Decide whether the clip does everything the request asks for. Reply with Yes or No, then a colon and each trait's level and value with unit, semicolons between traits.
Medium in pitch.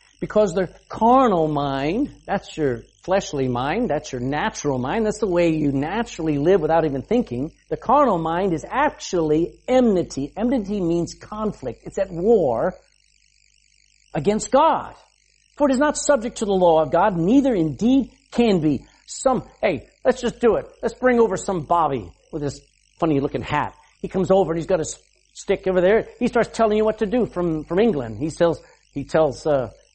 Yes: medium, 180 Hz